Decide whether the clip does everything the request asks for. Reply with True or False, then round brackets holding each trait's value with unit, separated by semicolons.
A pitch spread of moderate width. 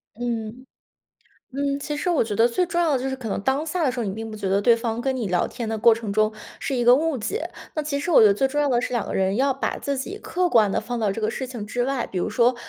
True (4.2 semitones)